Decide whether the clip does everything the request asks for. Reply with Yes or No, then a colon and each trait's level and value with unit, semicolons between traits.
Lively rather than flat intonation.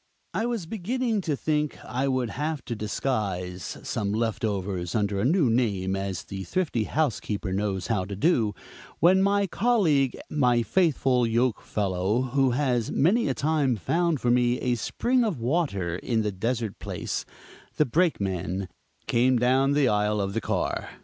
Yes: wide, 6.7 semitones